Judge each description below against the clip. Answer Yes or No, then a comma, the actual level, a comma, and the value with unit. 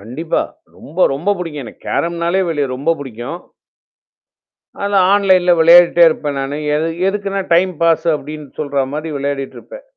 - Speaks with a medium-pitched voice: Yes, medium, 160 Hz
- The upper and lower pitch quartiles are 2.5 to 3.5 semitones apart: No, average, 3.9 semitones